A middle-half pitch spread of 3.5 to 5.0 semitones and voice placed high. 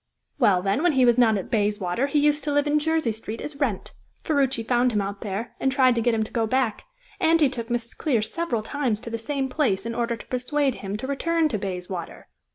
Yes: average, 4.7 semitones; high, 240 Hz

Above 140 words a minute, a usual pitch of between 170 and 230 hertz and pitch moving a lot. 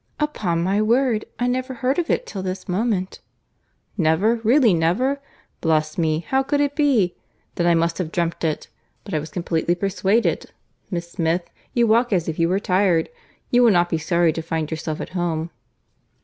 Yes: average, 170 wpm; medium, 185 Hz; wide, 5.9 semitones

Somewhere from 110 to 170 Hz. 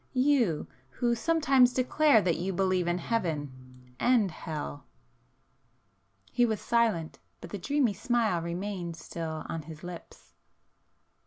No: medium, 185 Hz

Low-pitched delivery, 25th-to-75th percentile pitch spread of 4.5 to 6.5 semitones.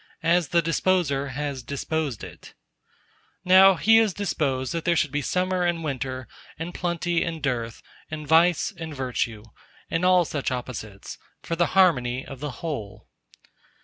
No: medium, 155 Hz; average, 4.8 semitones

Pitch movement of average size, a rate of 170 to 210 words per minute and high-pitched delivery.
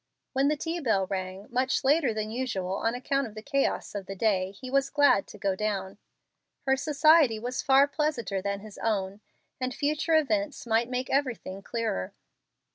No: wide, 5.7 semitones; average, 180 wpm; high, 240 Hz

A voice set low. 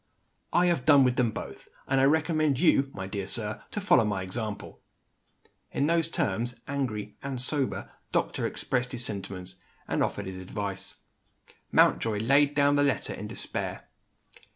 Yes: low, 125 Hz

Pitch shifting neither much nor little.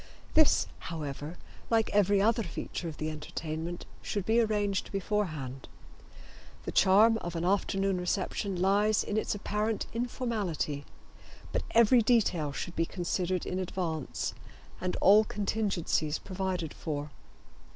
Yes: average, 4.2 semitones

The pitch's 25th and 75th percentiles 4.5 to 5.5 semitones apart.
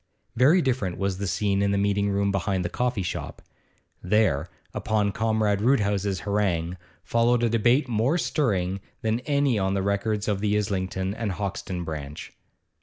No: average, 2.8 semitones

